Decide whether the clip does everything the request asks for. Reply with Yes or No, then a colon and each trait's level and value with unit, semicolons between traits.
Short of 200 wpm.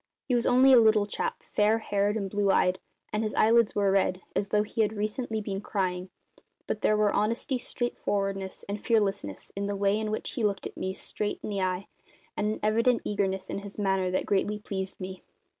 No: fast, 205 wpm